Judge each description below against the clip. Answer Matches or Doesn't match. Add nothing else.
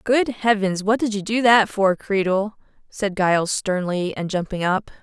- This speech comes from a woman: Matches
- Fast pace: Doesn't match